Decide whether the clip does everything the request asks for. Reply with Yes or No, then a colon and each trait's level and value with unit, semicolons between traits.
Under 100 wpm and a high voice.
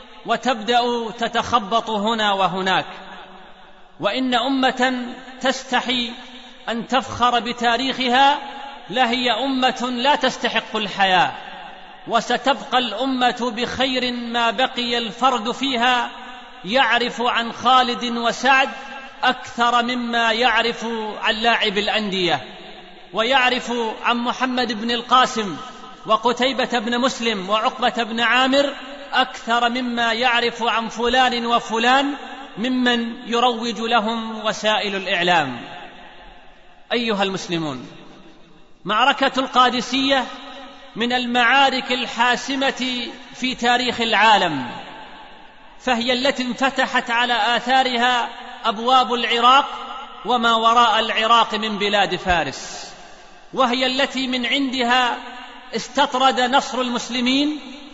Yes: average, 85 wpm; high, 245 Hz